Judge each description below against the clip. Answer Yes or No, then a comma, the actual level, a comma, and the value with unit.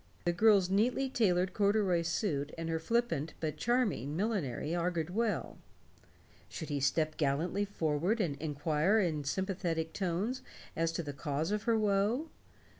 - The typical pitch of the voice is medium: Yes, medium, 175 Hz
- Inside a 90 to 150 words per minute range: Yes, average, 145 wpm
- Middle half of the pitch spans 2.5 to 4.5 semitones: No, average, 5.0 semitones